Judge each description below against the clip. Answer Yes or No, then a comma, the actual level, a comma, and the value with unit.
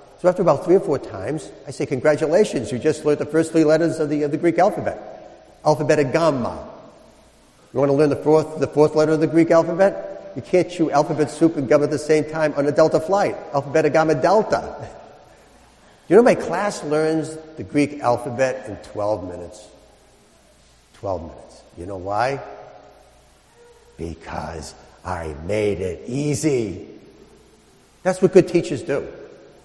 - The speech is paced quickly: No, average, 170 wpm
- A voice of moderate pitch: Yes, medium, 150 Hz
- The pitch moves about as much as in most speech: Yes, average, 4.1 semitones